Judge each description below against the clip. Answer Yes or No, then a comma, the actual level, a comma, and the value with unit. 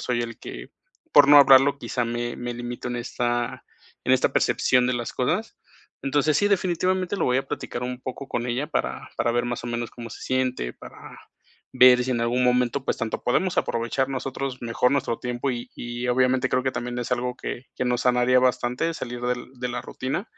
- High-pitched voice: No, low, 125 Hz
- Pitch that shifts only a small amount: Yes, narrow, 1.6 semitones